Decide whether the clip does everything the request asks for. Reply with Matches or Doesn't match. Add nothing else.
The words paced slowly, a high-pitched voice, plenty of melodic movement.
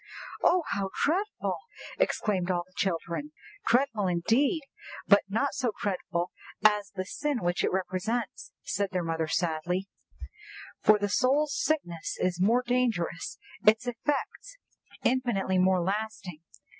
Matches